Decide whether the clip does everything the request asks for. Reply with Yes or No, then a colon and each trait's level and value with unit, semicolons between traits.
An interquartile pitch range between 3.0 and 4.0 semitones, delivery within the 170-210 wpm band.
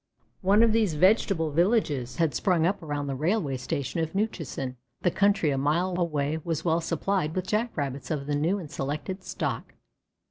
No: average, 4.7 semitones; average, 180 wpm